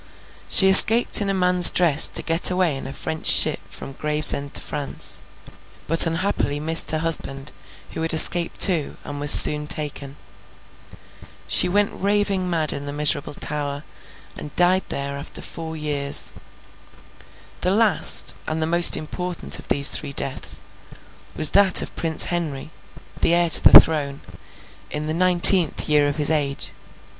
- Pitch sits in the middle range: Yes, medium, 160 Hz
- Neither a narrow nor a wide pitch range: Yes, average, 3.5 semitones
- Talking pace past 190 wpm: No, average, 155 wpm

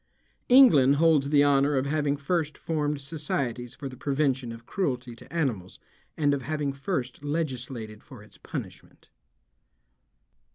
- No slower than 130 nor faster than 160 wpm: Yes, slow, 135 wpm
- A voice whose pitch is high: No, medium, 140 Hz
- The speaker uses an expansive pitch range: No, average, 2.8 semitones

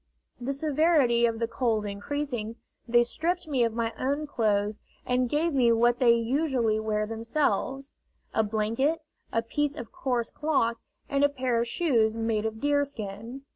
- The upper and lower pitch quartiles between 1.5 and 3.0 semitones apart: No, average, 4.1 semitones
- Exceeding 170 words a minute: No, average, 160 wpm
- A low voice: No, high, 240 Hz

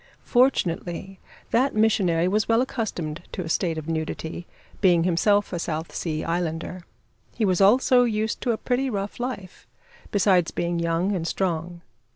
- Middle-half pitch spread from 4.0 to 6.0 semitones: Yes, average, 4.3 semitones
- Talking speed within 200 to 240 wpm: No, average, 155 wpm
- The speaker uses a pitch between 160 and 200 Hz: Yes, medium, 185 Hz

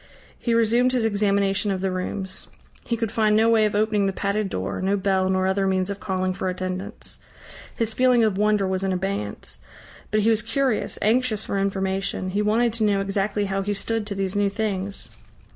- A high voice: Yes, high, 200 Hz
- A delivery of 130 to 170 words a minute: No, average, 200 wpm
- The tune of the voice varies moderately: No, narrow, 2.2 semitones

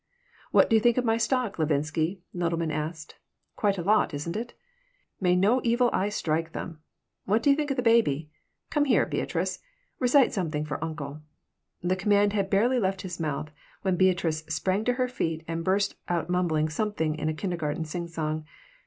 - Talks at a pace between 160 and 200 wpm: Yes, average, 180 wpm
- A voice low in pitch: No, medium, 180 Hz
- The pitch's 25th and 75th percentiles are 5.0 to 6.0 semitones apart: Yes, average, 5.3 semitones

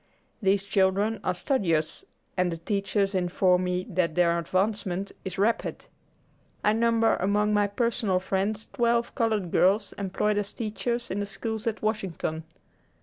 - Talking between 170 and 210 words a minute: No, average, 145 wpm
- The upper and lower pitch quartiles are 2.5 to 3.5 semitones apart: Yes, average, 2.9 semitones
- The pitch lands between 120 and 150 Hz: No, high, 200 Hz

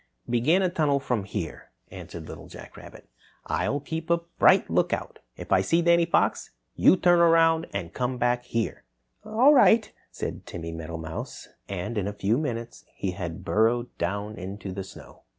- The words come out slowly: No, average, 170 wpm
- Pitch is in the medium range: No, low, 120 Hz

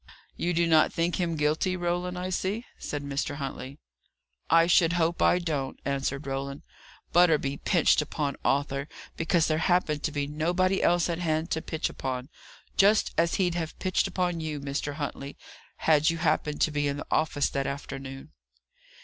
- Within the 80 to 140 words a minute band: No, average, 170 wpm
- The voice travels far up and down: No, average, 3.5 semitones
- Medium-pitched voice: Yes, medium, 155 Hz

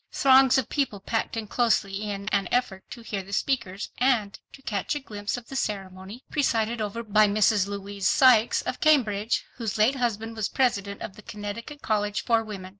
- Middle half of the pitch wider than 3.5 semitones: No, average, 3.2 semitones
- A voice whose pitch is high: Yes, high, 215 Hz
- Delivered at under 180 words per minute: No, average, 190 wpm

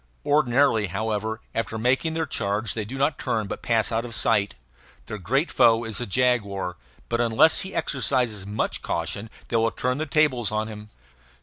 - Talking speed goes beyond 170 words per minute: Yes, average, 185 wpm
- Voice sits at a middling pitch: No, low, 115 Hz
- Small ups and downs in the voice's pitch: No, average, 3.1 semitones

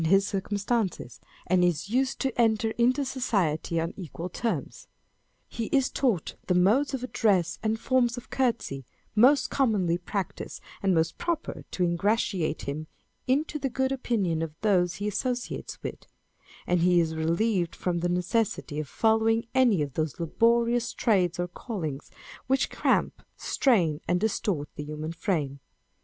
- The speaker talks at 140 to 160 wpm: Yes, average, 150 wpm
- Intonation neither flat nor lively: No, wide, 5.9 semitones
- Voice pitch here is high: Yes, high, 195 Hz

